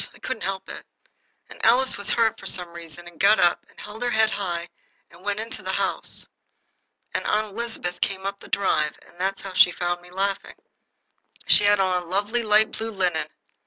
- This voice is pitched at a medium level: No, high, 195 Hz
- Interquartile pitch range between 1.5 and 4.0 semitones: Yes, average, 3.5 semitones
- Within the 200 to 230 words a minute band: Yes, fast, 205 wpm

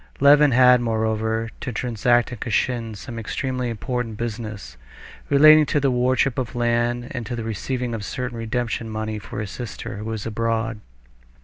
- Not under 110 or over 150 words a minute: No, average, 165 wpm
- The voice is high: No, low, 120 Hz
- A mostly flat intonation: Yes, narrow, 2.1 semitones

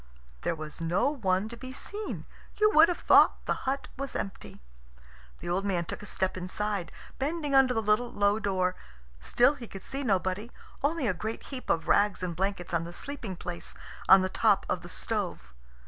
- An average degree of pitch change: No, wide, 6.2 semitones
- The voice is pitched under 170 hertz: No, high, 205 Hz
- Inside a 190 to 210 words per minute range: Yes, average, 195 wpm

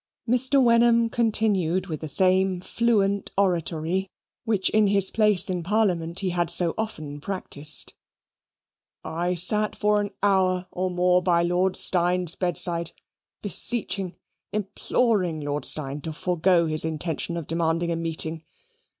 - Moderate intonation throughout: Yes, average, 3.4 semitones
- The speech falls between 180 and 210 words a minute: No, slow, 135 wpm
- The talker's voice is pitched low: No, medium, 180 Hz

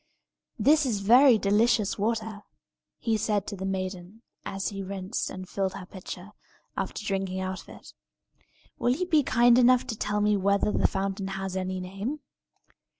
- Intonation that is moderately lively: Yes, average, 3.0 semitones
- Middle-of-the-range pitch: No, high, 200 Hz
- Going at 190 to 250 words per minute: No, average, 165 wpm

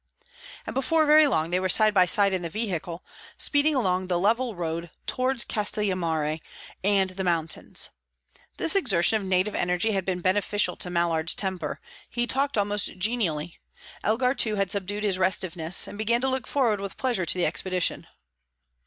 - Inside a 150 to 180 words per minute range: Yes, average, 170 wpm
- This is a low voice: No, high, 195 Hz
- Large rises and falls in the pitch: No, average, 4.0 semitones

